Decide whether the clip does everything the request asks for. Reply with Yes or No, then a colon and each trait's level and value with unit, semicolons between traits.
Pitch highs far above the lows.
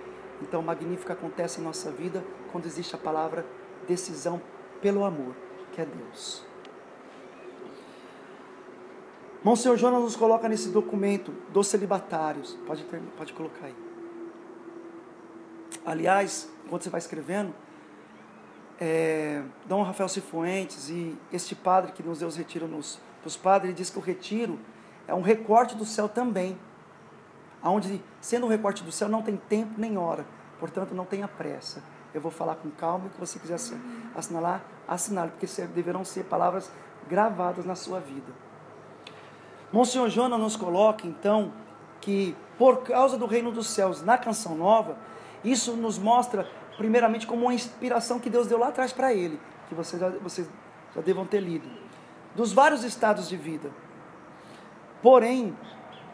No: average, 4.9 semitones